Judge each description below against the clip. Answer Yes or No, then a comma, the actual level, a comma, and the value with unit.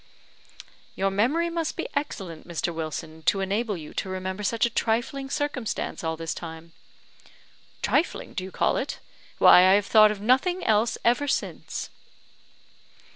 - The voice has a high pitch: Yes, high, 205 Hz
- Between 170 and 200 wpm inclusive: No, average, 150 wpm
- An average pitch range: No, wide, 5.7 semitones